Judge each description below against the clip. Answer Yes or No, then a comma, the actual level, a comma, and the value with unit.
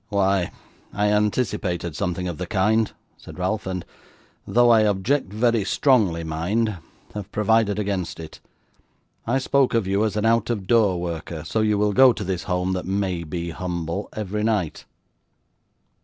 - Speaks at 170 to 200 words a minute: No, average, 160 wpm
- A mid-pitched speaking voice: No, low, 100 Hz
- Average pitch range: Yes, average, 3.4 semitones